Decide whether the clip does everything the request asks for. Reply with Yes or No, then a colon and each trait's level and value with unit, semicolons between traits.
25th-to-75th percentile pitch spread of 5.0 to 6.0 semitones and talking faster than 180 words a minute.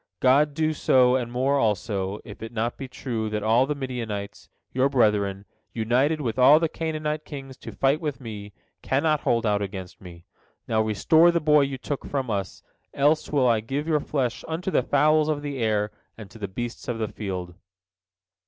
Yes: average, 5.3 semitones; average, 190 wpm